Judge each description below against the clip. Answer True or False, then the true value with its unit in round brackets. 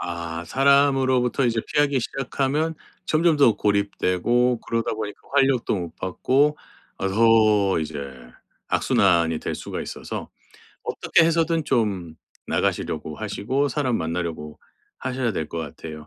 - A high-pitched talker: False (115 Hz)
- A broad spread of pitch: True (7.5 semitones)